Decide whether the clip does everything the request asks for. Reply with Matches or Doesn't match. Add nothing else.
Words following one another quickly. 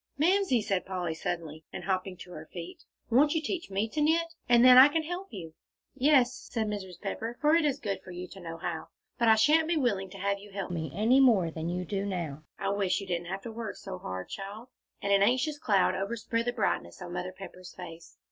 Matches